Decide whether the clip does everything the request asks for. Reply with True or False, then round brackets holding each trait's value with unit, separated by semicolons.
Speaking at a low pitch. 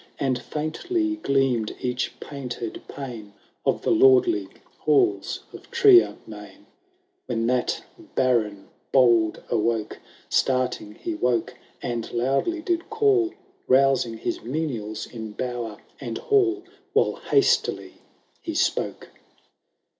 True (130 Hz)